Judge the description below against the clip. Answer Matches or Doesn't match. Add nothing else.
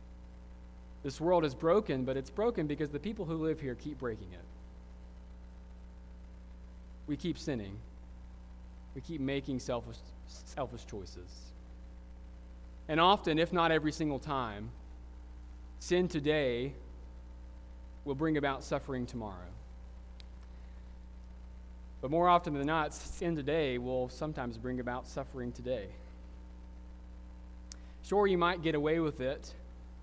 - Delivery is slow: Matches